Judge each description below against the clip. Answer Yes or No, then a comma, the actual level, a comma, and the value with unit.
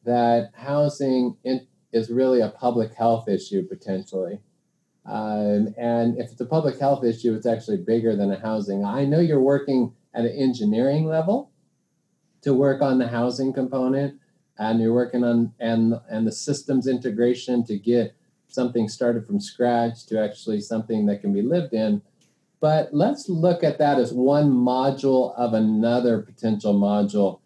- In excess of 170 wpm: No, average, 155 wpm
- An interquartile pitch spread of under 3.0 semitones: No, average, 3.6 semitones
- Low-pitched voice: Yes, low, 120 Hz